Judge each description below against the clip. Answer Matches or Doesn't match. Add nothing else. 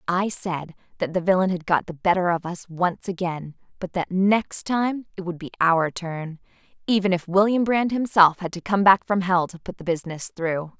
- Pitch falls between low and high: Matches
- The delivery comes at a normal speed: Doesn't match